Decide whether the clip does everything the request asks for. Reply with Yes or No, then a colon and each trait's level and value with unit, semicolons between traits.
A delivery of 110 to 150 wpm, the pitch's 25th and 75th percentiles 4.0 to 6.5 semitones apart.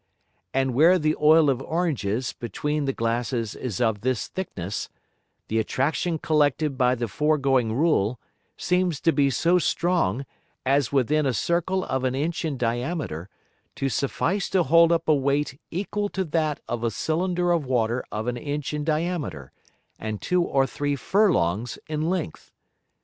No: average, 160 wpm; average, 5.2 semitones